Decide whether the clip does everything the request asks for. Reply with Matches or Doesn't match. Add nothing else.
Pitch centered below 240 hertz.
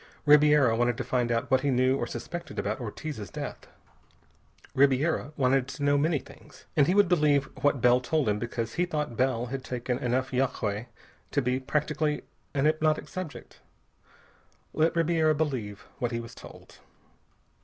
Matches